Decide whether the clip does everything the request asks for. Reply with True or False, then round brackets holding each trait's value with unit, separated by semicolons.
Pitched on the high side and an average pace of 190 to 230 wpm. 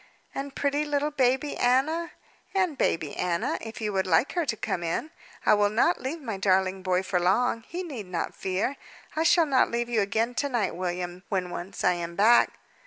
True (225 Hz; 200 wpm)